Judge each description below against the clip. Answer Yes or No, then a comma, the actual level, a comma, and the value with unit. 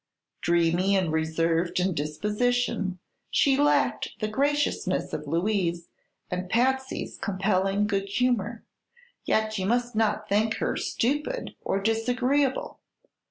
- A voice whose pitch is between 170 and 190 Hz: No, high, 210 Hz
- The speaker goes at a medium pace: No, slow, 115 wpm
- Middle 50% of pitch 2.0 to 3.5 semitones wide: No, average, 5.0 semitones